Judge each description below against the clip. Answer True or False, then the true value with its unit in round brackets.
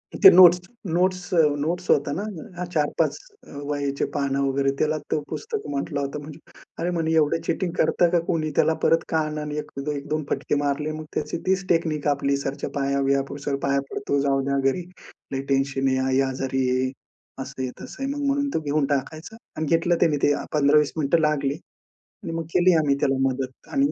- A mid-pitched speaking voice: True (150 Hz)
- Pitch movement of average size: True (3.3 semitones)